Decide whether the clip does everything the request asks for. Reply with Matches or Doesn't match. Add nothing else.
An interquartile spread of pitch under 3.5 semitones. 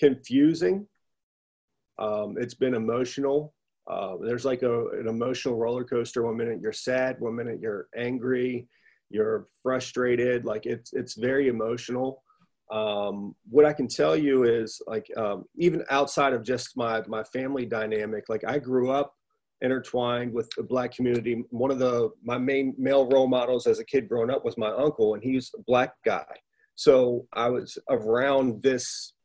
Matches